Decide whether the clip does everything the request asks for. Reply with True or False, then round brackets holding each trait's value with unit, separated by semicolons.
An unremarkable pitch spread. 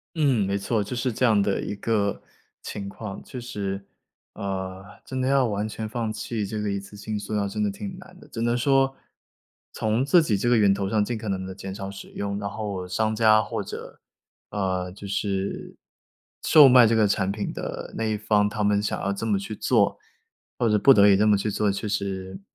False (2.3 semitones)